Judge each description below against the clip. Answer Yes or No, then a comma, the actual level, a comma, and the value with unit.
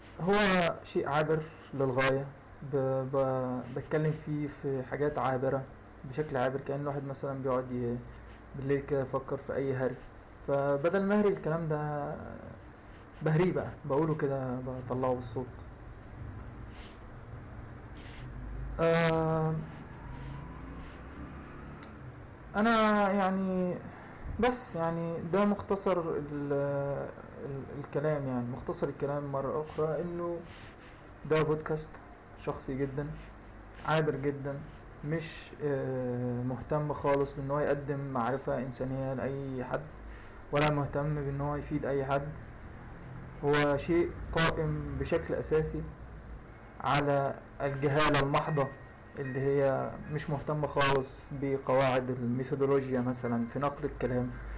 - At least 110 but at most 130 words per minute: No, average, 95 wpm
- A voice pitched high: No, medium, 140 Hz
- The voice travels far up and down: No, average, 3.1 semitones